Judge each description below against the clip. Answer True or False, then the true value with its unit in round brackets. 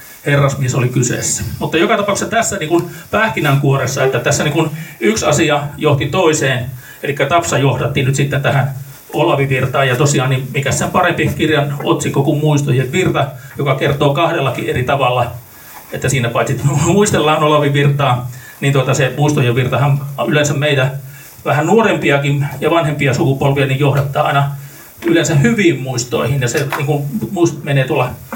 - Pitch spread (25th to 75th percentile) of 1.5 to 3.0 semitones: True (2.5 semitones)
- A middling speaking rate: True (145 wpm)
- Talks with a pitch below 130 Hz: False (140 Hz)